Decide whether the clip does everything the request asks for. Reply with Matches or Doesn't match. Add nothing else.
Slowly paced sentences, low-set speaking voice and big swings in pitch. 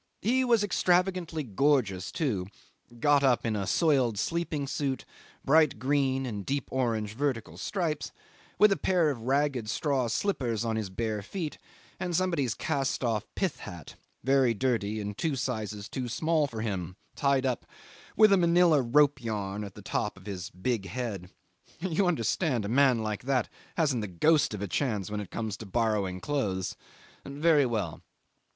Doesn't match